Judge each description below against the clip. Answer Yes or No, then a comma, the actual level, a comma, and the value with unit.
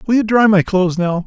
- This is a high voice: Yes, high, 195 Hz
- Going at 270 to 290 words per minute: Yes, fast, 285 wpm